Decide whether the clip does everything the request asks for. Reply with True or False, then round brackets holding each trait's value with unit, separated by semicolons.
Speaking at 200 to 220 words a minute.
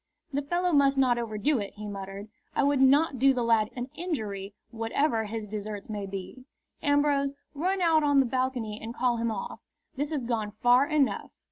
False (190 wpm)